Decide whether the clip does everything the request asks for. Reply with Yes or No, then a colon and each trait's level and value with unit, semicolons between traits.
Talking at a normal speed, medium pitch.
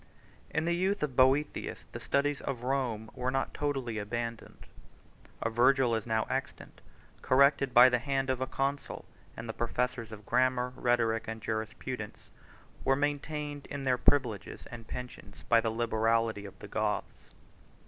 No: average, 160 wpm; low, 125 Hz